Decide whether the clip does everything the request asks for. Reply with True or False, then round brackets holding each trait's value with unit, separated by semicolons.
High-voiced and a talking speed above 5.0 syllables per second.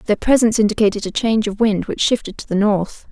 True (210 Hz; 6.4 syllables/s)